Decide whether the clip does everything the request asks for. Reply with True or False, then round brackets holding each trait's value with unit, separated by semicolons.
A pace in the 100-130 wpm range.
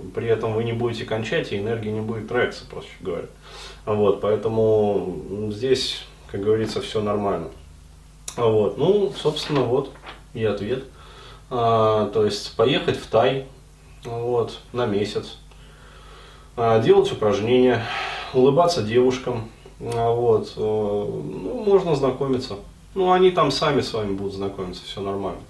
True (125 wpm)